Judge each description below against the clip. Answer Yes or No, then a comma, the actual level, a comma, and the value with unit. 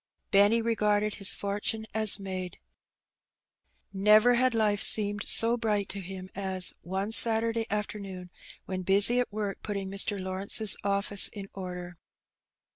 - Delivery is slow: Yes, slow, 130 wpm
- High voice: Yes, high, 205 Hz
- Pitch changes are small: Yes, narrow, 2.1 semitones